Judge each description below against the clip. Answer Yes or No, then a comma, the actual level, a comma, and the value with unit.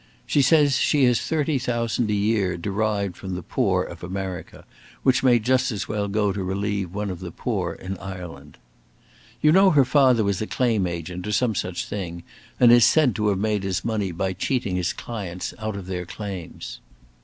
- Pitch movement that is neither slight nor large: Yes, average, 4.5 semitones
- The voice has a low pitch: Yes, low, 100 Hz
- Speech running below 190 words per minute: No, average, 195 wpm